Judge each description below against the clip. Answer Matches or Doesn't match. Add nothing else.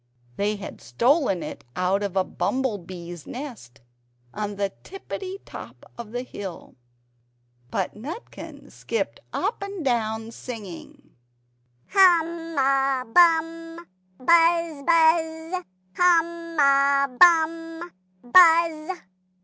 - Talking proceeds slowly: Matches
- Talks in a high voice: Matches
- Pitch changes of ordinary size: Doesn't match